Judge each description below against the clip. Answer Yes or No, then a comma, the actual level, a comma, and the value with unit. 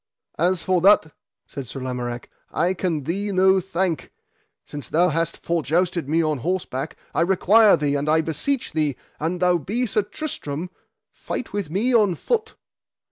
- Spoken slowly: No, average, 165 wpm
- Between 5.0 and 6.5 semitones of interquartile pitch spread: No, average, 4.0 semitones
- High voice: No, medium, 170 Hz